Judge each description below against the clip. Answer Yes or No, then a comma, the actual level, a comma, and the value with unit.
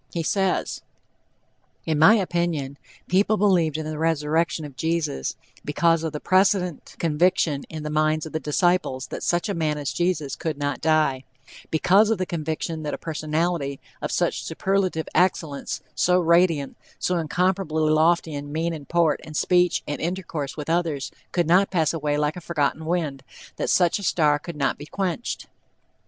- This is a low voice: No, medium, 160 Hz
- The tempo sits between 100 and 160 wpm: No, average, 170 wpm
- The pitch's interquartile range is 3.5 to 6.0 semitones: No, average, 2.8 semitones